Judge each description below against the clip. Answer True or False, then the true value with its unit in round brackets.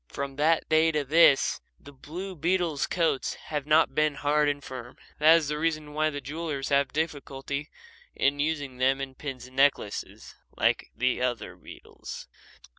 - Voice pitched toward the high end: False (145 Hz)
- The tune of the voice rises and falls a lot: False (2.6 semitones)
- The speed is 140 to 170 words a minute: True (160 wpm)